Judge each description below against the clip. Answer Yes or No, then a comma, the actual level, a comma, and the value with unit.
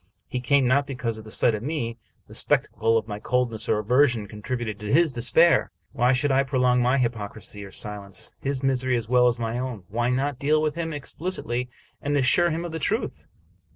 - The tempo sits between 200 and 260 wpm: Yes, fast, 205 wpm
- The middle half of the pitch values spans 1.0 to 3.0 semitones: No, average, 3.7 semitones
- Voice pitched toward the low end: Yes, low, 125 Hz